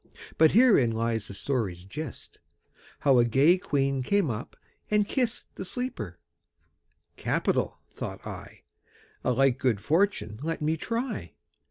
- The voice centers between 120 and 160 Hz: Yes, medium, 140 Hz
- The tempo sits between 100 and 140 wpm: Yes, slow, 135 wpm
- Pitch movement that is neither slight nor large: No, wide, 8.5 semitones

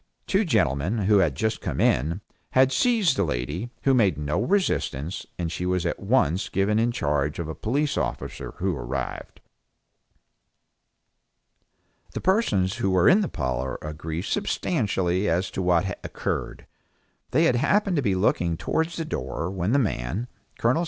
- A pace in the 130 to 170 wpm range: Yes, average, 160 wpm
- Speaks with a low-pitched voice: Yes, very low, 95 Hz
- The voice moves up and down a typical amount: No, wide, 7.7 semitones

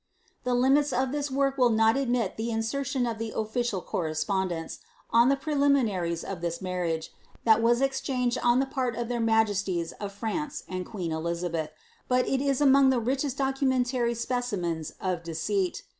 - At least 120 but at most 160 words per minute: No, average, 175 wpm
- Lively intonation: Yes, wide, 6.0 semitones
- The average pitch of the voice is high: Yes, high, 235 Hz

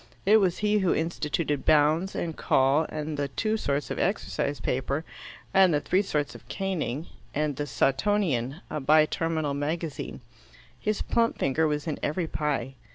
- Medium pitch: Yes, medium, 155 Hz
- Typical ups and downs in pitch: Yes, average, 3.7 semitones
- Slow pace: No, average, 160 wpm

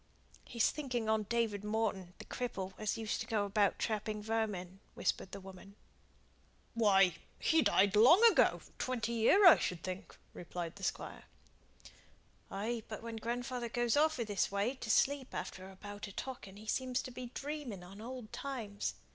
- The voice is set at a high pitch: Yes, high, 220 Hz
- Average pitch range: Yes, average, 3.5 semitones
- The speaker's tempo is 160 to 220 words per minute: Yes, average, 170 wpm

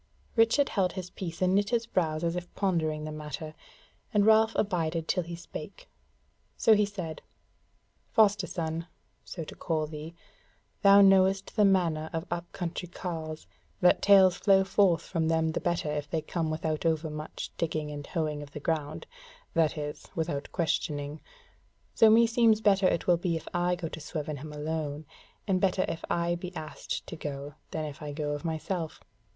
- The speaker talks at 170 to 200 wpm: Yes, average, 175 wpm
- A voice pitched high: No, medium, 165 Hz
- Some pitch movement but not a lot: Yes, average, 3.5 semitones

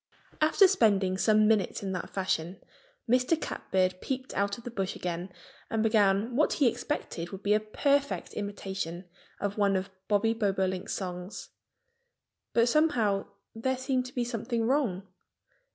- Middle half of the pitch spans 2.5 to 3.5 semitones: No, average, 4.3 semitones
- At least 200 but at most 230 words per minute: No, average, 150 wpm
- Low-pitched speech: No, high, 210 Hz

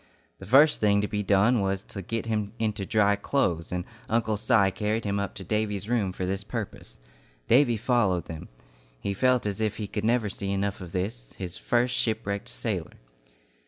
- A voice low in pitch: Yes, low, 105 Hz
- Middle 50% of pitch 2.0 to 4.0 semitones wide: Yes, narrow, 2.6 semitones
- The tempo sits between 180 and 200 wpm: Yes, average, 190 wpm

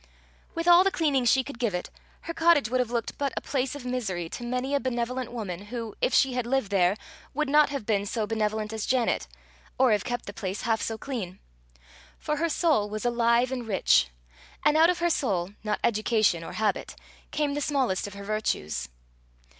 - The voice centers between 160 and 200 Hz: No, high, 235 Hz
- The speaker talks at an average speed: No, fast, 210 wpm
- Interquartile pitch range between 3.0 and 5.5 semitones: Yes, average, 4.6 semitones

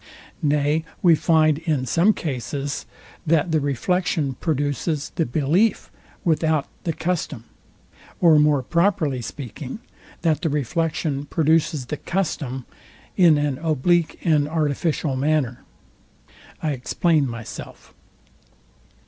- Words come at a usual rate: No, slow, 105 wpm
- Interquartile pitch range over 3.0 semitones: No, average, 2.7 semitones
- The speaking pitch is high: No, medium, 150 Hz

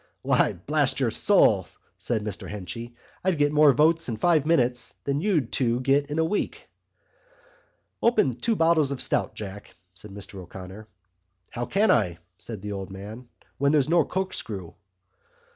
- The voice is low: Yes, low, 125 Hz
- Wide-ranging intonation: Yes, wide, 7.0 semitones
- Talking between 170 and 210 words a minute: No, average, 160 wpm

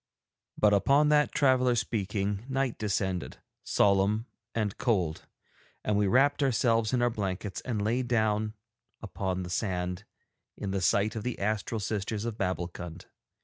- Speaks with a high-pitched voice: No, low, 105 Hz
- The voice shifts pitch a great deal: No, average, 3.4 semitones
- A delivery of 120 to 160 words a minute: Yes, average, 145 wpm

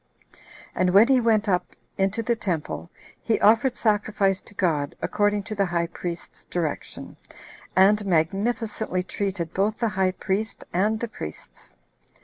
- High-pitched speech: Yes, high, 200 Hz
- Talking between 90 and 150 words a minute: Yes, average, 140 wpm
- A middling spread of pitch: Yes, average, 3.2 semitones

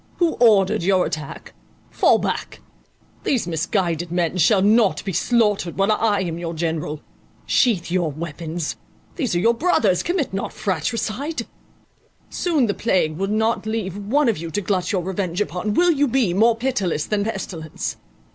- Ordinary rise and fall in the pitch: Yes, average, 4.8 semitones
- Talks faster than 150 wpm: Yes, average, 160 wpm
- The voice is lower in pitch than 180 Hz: No, high, 195 Hz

